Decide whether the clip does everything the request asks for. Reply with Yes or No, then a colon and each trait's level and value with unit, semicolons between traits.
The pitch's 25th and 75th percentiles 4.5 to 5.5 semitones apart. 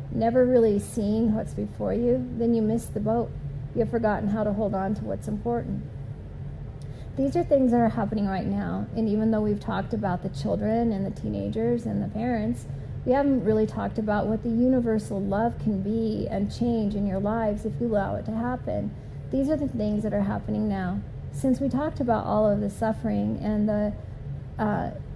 Yes: average, 5.2 semitones